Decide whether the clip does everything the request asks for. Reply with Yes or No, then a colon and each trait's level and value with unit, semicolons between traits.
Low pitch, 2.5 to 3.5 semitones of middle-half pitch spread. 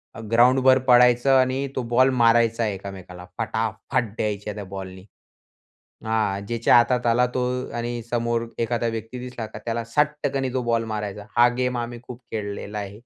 Yes: low, 115 Hz; average, 2.8 semitones